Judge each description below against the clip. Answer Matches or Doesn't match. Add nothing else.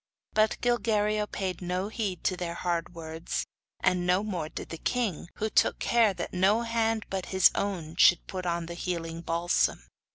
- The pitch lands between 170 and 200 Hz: Matches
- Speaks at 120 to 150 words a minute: Doesn't match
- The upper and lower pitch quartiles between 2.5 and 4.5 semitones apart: Matches